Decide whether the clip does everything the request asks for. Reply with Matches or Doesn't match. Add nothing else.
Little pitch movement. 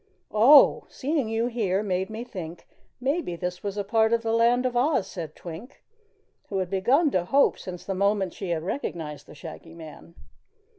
Doesn't match